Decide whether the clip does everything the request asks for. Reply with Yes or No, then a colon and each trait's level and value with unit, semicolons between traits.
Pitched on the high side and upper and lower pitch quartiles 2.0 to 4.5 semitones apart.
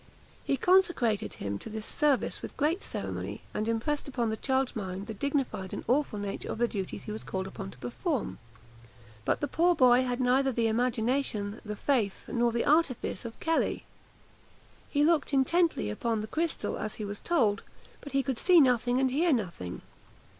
No: high, 245 Hz; average, 4.9 semitones